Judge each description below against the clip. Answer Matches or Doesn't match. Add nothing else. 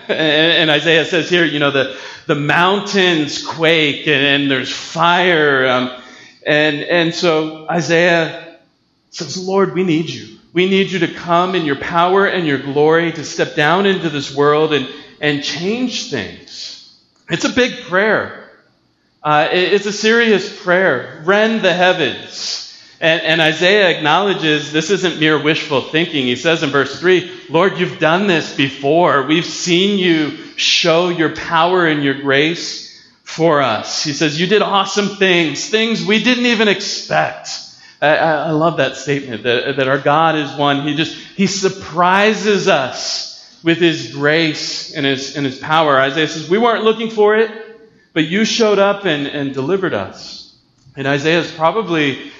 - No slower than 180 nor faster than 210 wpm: Doesn't match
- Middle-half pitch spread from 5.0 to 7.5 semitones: Doesn't match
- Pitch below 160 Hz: Doesn't match